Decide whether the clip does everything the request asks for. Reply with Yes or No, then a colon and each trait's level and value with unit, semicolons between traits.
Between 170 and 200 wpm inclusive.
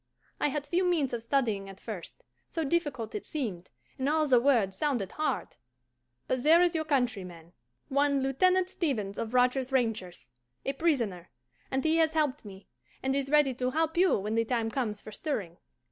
Yes: average, 180 wpm